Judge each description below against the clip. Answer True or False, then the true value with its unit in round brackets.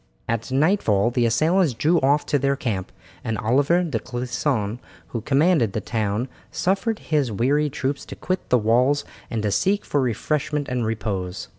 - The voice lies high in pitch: False (130 Hz)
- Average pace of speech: True (165 wpm)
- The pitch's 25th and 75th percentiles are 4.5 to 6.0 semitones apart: True (5.0 semitones)